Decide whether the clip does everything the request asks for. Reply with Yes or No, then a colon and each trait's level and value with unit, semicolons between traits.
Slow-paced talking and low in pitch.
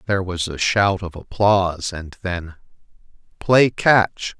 Yes: slow, 125 wpm; very low, 95 Hz